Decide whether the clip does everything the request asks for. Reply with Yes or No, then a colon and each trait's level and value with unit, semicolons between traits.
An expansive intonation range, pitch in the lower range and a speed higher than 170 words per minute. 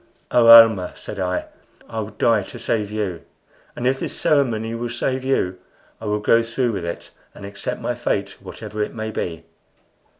No: average, 2.8 semitones; low, 110 Hz; average, 180 wpm